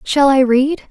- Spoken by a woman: Yes, female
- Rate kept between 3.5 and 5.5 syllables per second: Yes, 4.1 syllables/s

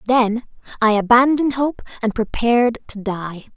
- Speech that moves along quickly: No, slow, 135 wpm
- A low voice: No, high, 235 Hz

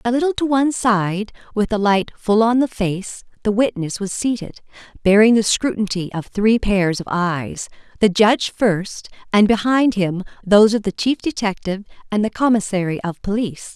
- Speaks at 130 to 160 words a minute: No, average, 170 wpm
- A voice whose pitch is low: No, high, 210 Hz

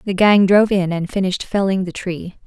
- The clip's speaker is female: Yes, female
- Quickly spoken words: Yes, fast, 220 wpm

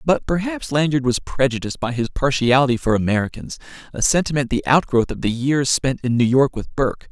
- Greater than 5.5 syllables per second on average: Yes, 5.8 syllables/s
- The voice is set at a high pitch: No, low, 135 Hz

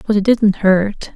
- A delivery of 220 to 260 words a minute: No, fast, 205 wpm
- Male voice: No, female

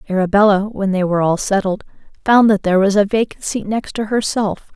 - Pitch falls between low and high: No, high, 200 Hz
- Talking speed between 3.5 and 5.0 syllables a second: No, 5.5 syllables/s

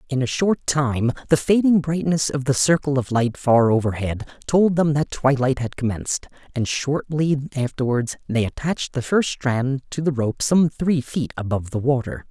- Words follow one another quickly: No, average, 180 wpm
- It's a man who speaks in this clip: Yes, male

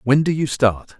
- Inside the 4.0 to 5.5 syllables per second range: Yes, 4.6 syllables/s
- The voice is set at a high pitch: No, low, 135 Hz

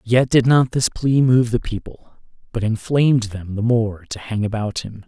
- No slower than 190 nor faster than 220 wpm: Yes, average, 200 wpm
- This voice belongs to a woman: No, male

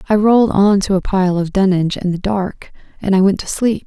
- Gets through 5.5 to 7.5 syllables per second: Yes, 5.7 syllables/s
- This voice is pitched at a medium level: No, high, 195 Hz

